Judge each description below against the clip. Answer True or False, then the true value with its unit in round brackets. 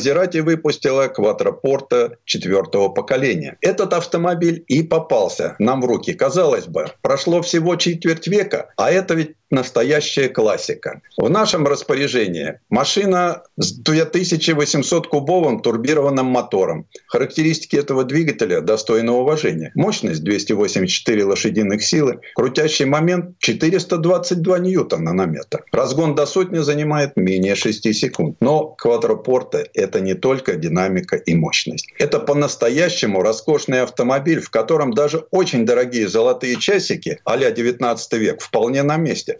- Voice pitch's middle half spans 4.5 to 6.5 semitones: True (5.4 semitones)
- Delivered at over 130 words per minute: False (120 wpm)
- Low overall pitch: False (155 Hz)